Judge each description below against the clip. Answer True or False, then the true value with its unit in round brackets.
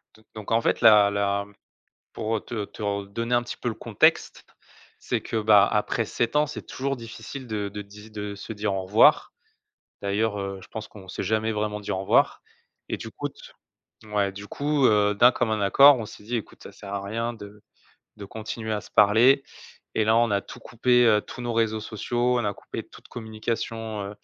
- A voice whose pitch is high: False (110 Hz)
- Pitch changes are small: True (2.2 semitones)